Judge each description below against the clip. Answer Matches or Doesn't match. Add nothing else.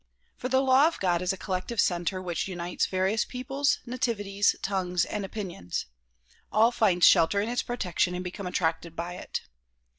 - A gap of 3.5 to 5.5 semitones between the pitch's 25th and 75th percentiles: Matches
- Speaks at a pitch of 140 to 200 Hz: Matches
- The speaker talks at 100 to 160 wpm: Doesn't match